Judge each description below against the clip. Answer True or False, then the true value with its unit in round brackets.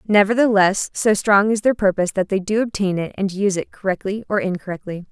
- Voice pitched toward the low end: False (200 Hz)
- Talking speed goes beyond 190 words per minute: True (200 wpm)